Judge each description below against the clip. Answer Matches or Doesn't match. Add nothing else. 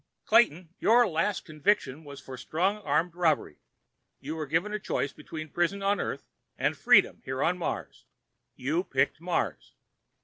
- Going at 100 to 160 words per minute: Matches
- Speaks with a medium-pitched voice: Matches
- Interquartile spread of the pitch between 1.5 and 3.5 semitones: Doesn't match